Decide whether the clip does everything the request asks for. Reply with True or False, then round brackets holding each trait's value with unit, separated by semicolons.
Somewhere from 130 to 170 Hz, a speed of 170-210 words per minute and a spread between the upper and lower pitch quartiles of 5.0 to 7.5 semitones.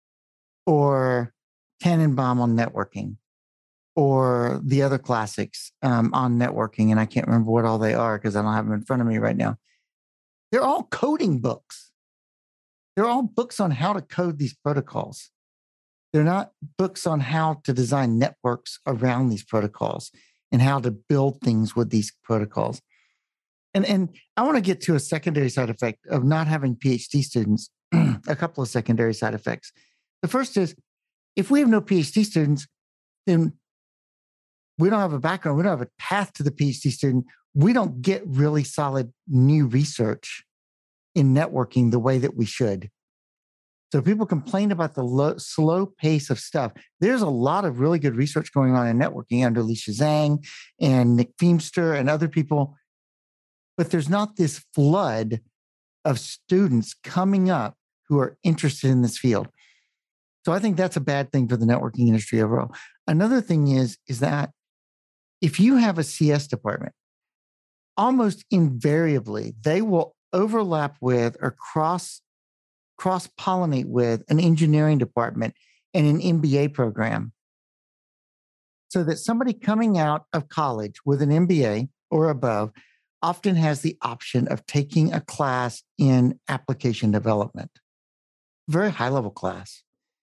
False (140 Hz; 155 wpm; 5.6 semitones)